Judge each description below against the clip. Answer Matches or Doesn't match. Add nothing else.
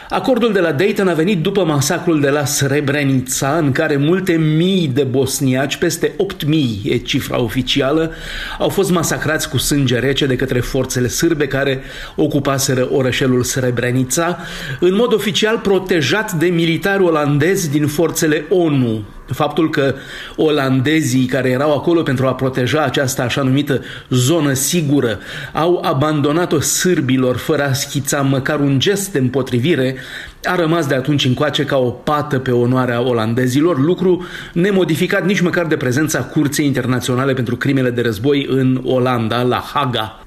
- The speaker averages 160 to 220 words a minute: Doesn't match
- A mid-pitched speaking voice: Matches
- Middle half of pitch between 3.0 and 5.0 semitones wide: Matches